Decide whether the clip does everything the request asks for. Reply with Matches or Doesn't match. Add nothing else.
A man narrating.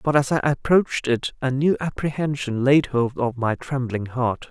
Matches